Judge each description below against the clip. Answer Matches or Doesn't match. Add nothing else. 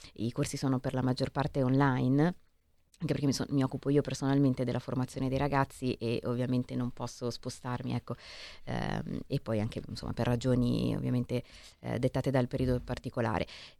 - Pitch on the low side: Matches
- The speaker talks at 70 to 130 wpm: Doesn't match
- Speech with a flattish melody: Matches